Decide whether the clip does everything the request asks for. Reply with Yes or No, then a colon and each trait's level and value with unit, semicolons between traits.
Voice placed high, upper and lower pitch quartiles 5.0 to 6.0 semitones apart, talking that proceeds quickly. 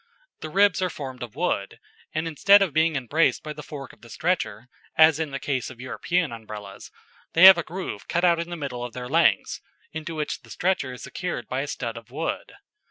No: medium, 150 Hz; average, 5.3 semitones; fast, 220 wpm